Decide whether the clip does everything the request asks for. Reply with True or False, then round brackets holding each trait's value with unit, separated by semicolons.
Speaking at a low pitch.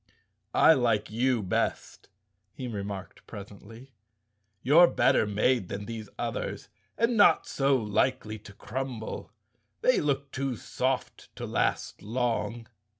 True (120 Hz)